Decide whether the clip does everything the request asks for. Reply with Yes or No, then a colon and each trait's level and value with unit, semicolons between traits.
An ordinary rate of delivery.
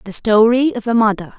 No: fast, 215 wpm